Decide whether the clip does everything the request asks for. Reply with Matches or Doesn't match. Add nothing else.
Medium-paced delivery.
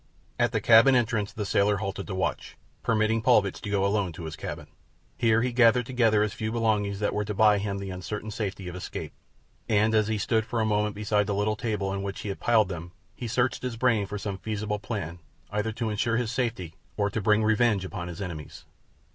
Doesn't match